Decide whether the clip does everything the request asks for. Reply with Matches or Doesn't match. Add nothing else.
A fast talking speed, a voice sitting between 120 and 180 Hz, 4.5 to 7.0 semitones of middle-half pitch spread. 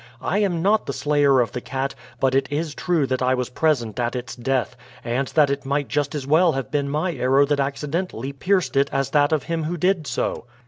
Doesn't match